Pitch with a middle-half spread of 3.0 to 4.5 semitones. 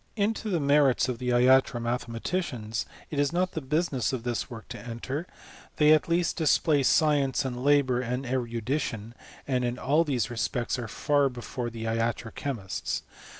Yes: average, 3.7 semitones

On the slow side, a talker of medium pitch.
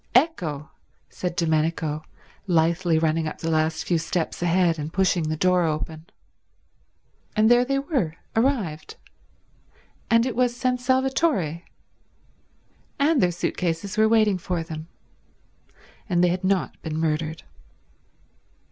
Yes: slow, 130 wpm; medium, 175 Hz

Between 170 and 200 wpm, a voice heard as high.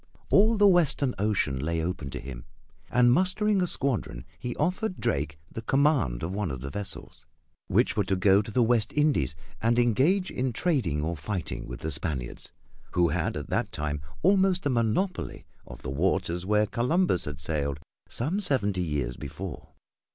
No: average, 175 wpm; low, 105 Hz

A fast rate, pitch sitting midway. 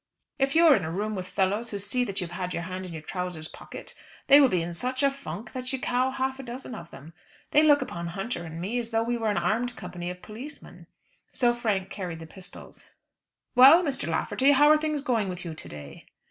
No: fast, 240 wpm; high, 215 Hz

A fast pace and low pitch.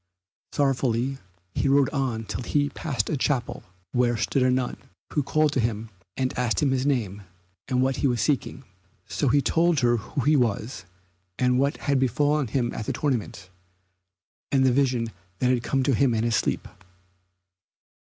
No: average, 175 wpm; low, 130 Hz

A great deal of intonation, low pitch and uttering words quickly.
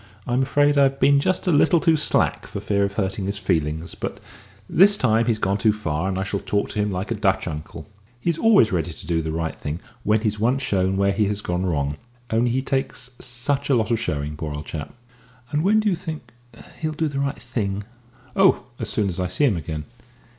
Yes: wide, 6.9 semitones; low, 105 Hz; fast, 230 wpm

